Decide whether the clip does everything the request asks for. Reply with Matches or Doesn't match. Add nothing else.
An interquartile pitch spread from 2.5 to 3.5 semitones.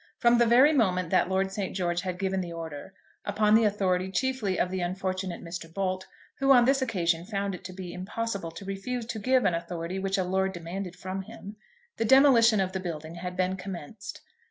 Matches